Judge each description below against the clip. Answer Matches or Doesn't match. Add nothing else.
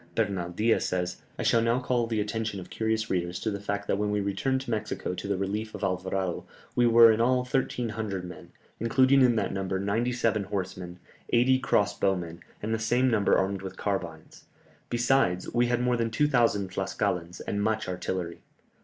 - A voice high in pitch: Doesn't match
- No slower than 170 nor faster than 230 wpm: Matches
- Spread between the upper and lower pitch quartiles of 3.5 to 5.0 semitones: Matches